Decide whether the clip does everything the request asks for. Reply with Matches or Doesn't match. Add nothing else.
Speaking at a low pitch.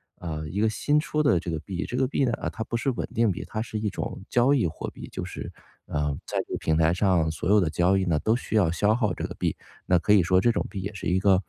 Matches